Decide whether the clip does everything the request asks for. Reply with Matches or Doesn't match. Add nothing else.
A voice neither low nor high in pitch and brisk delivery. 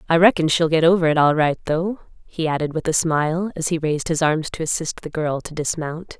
Matches